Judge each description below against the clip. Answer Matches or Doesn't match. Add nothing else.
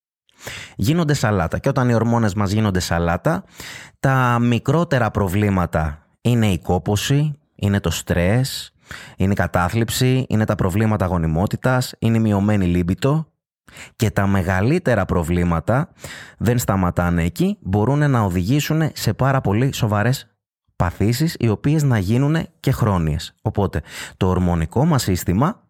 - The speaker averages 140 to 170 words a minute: Doesn't match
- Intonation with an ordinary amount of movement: Doesn't match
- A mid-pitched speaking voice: Doesn't match